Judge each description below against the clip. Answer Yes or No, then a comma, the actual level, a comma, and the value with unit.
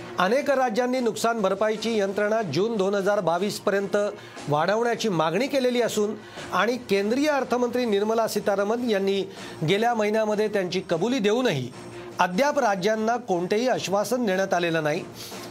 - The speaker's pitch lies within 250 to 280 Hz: No, high, 210 Hz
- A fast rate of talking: No, average, 120 wpm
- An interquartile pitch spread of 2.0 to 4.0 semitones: Yes, average, 3.3 semitones